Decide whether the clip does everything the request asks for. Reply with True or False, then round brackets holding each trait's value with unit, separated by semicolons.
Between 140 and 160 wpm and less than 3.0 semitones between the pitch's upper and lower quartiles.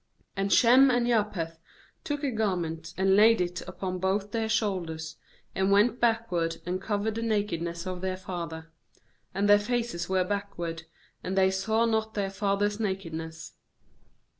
False (150 wpm; 3.9 semitones)